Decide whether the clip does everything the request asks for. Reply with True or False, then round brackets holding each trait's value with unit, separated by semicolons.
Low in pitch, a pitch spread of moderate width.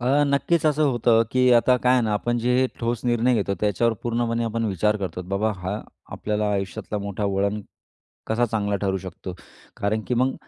True (110 Hz; 3.0 semitones)